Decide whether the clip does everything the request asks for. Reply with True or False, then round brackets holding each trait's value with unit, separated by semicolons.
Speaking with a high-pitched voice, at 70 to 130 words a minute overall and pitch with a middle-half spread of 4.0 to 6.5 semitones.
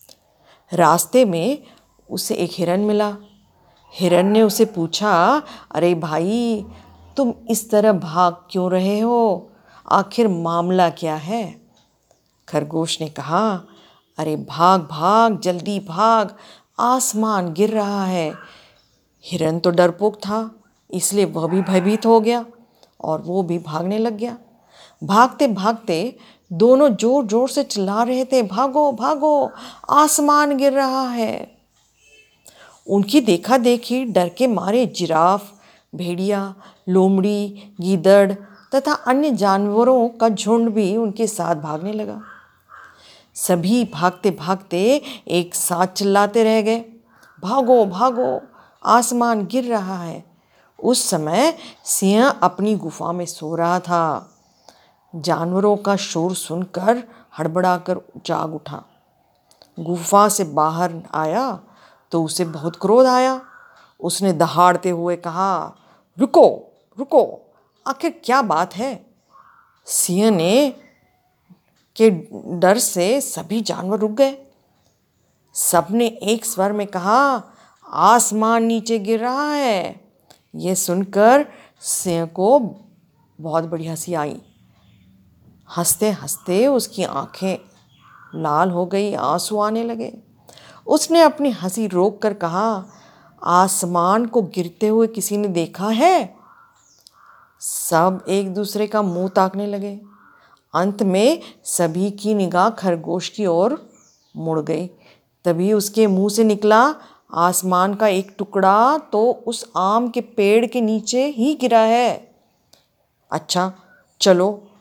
True (205 Hz; 115 wpm; 4.5 semitones)